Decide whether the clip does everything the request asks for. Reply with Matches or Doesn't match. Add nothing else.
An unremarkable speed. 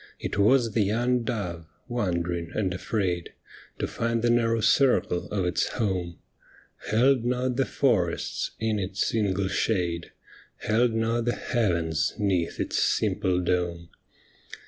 Doesn't match